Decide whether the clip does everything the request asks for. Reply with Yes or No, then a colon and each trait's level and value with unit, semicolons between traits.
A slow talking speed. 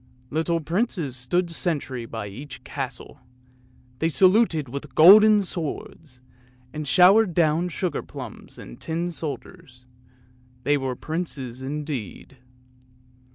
Yes: slow, 110 wpm